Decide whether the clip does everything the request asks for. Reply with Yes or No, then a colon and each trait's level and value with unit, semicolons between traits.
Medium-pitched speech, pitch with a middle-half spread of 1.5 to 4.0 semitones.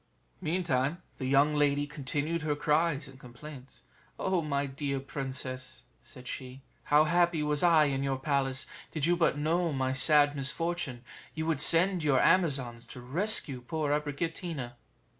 Yes: medium, 145 Hz; average, 3.5 semitones